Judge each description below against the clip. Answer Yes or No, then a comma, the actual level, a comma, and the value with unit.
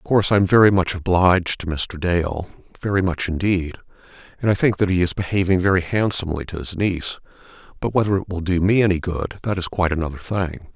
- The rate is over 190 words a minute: Yes, average, 200 wpm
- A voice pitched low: Yes, very low, 90 Hz